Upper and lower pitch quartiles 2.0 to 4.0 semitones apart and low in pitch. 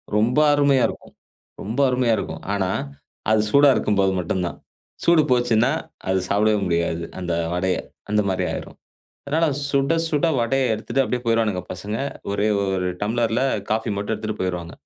No: average, 4.7 semitones; low, 110 Hz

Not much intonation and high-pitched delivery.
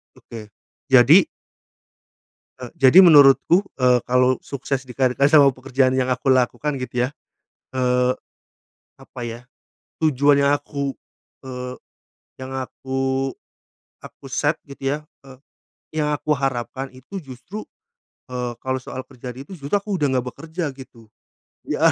No: narrow, 2.1 semitones; low, 130 Hz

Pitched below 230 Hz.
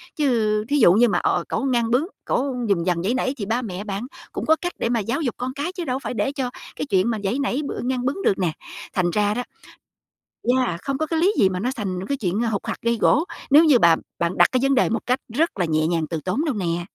No: high, 235 Hz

